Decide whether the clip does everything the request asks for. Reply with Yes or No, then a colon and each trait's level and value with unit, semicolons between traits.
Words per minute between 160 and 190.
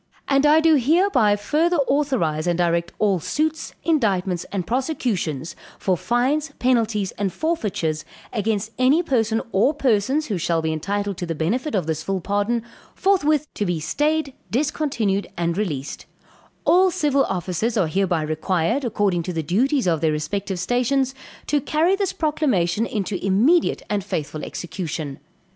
No: average, 150 wpm